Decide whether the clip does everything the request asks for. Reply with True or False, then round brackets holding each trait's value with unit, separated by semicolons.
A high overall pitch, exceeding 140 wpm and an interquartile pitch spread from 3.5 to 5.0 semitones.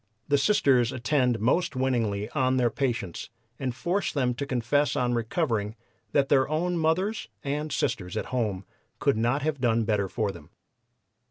False (125 Hz; 160 wpm; 4.2 semitones)